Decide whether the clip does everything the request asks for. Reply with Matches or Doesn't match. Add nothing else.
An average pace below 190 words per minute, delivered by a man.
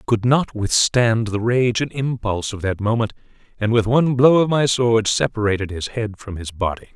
Doesn't match